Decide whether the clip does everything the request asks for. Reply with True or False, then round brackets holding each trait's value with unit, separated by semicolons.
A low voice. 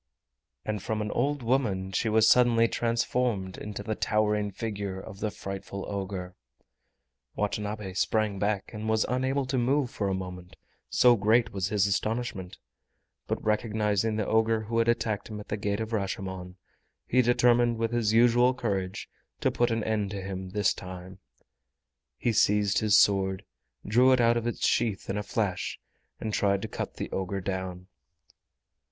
True (105 Hz)